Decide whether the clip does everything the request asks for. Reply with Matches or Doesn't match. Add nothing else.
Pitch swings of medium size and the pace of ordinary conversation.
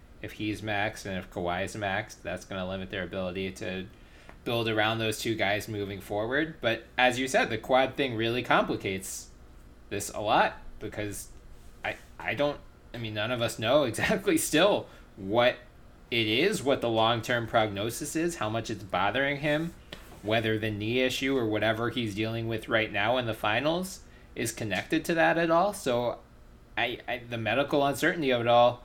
Matches